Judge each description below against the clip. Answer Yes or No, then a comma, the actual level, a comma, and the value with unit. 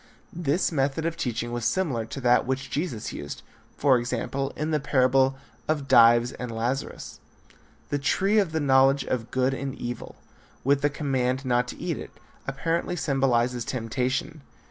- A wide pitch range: No, average, 2.8 semitones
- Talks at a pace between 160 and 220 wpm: Yes, average, 165 wpm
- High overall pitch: No, low, 135 Hz